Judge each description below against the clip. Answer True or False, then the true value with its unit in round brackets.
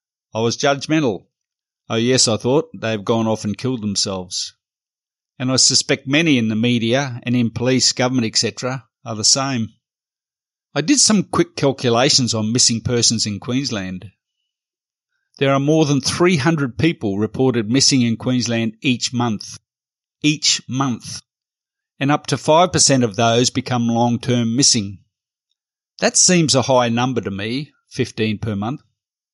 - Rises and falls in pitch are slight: False (3.3 semitones)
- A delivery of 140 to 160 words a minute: True (150 wpm)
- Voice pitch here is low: True (125 Hz)